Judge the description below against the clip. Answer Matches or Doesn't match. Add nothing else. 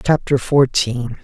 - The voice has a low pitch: Matches